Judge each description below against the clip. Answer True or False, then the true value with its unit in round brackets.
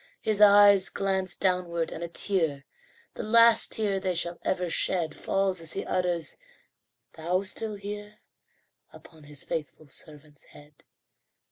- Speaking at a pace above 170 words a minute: False (135 wpm)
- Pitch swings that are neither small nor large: True (3.8 semitones)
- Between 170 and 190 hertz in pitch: True (185 Hz)